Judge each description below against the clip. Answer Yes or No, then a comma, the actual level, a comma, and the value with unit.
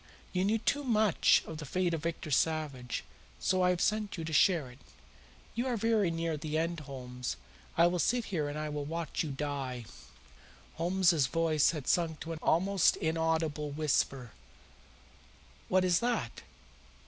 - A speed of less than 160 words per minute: No, average, 165 wpm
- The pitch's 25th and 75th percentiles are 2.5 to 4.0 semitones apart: Yes, average, 3.7 semitones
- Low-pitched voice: No, medium, 165 Hz